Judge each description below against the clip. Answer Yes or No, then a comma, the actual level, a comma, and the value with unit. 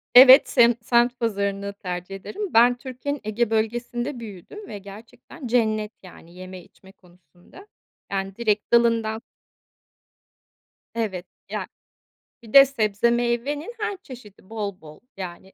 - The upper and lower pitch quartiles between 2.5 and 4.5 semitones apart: Yes, average, 3.8 semitones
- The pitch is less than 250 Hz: Yes, high, 225 Hz